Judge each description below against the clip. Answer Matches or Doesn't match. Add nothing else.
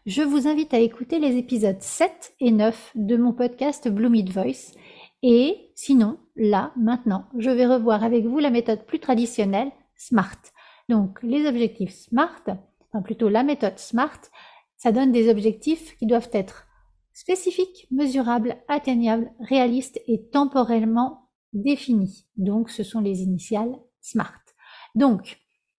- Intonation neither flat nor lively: Matches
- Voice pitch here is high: Matches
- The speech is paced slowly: Matches